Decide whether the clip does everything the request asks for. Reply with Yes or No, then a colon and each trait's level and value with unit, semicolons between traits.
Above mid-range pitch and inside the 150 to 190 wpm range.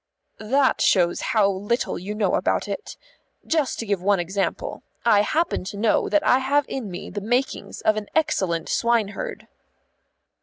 Yes: high, 215 Hz; average, 160 wpm